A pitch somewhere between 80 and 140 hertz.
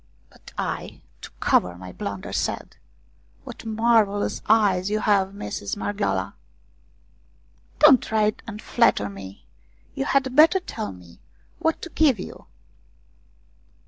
No: high, 205 Hz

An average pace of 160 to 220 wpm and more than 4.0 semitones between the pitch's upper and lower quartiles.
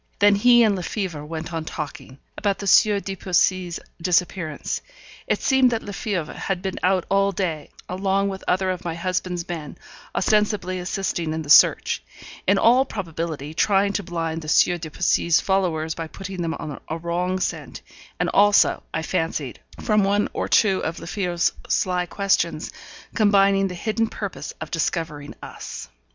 No: average, 165 wpm; average, 3.2 semitones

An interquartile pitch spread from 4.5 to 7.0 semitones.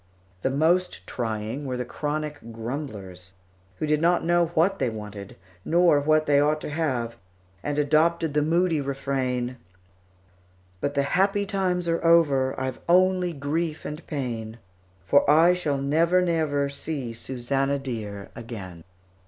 Yes: average, 4.9 semitones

